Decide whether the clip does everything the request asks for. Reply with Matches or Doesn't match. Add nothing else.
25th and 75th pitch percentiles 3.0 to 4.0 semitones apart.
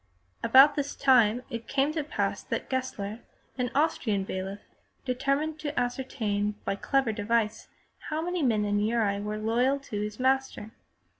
Doesn't match